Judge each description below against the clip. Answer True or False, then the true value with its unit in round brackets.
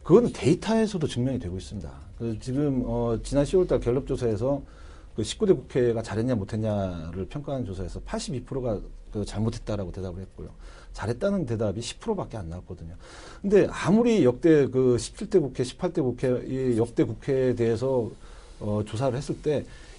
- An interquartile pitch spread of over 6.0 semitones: False (5.3 semitones)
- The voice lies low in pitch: True (120 Hz)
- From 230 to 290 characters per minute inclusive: False (335 characters per minute)